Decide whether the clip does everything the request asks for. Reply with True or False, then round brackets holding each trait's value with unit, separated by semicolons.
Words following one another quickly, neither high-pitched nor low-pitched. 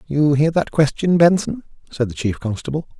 False (180 wpm; 145 Hz)